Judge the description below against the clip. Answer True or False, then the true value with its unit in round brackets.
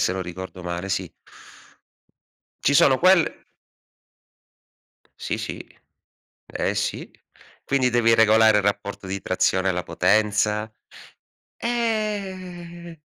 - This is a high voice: False (110 Hz)